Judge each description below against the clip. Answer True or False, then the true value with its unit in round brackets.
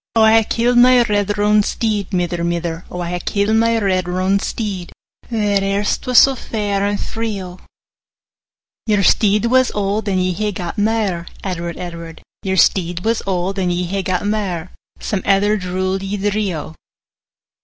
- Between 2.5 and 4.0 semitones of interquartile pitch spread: True (2.9 semitones)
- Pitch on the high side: True (200 Hz)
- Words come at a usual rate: True (180 wpm)